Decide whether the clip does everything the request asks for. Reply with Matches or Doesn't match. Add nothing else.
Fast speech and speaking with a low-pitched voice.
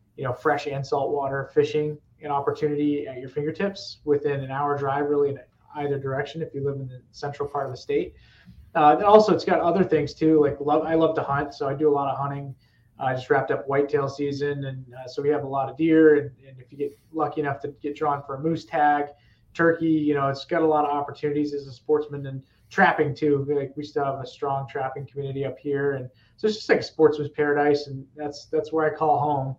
Doesn't match